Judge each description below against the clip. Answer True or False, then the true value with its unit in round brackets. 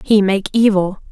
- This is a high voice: True (200 Hz)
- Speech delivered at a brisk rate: False (160 wpm)